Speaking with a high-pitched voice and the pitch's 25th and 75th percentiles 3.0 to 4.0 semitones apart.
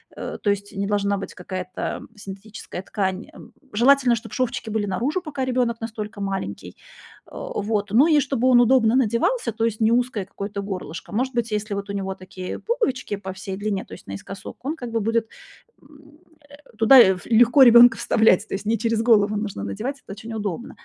Yes: high, 220 Hz; average, 3.5 semitones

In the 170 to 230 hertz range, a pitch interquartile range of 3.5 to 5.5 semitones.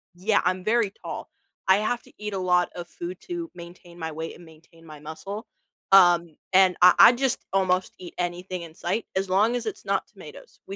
No: medium, 185 Hz; average, 3.1 semitones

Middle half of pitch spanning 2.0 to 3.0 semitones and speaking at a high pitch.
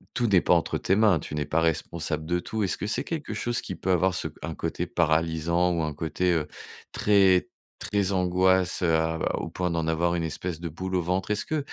No: narrow, 2.5 semitones; very low, 90 Hz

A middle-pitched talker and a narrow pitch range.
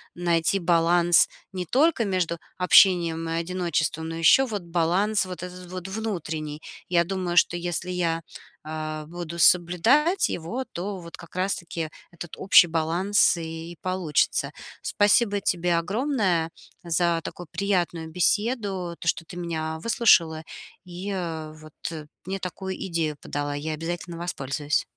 Yes: medium, 175 Hz; narrow, 2.3 semitones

